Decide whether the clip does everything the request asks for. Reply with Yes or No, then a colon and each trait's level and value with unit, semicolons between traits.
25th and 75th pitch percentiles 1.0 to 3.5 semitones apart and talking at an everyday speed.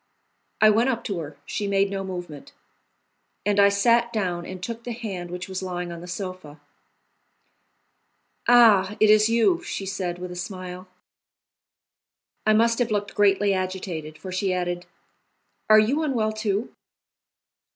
Yes: average, 3.1 semitones; average, 150 wpm